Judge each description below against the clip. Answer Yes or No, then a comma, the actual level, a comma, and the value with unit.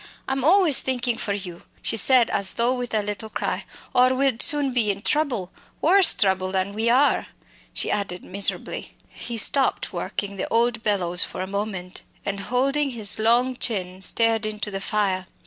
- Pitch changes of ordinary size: Yes, average, 4.2 semitones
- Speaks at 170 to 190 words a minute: Yes, average, 175 wpm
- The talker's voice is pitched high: Yes, high, 220 Hz